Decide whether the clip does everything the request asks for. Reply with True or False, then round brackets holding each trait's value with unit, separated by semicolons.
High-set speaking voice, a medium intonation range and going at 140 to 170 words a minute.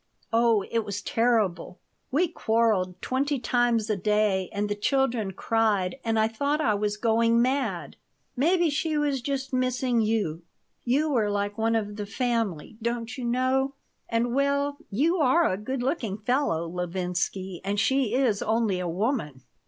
True (230 Hz; 4.4 semitones; 160 wpm)